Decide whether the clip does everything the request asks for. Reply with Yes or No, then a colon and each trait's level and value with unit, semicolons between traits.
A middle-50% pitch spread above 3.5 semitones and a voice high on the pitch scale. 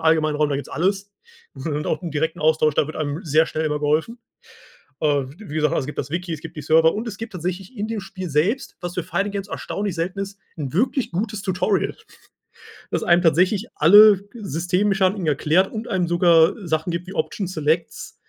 No: average, 4.1 semitones; medium, 175 Hz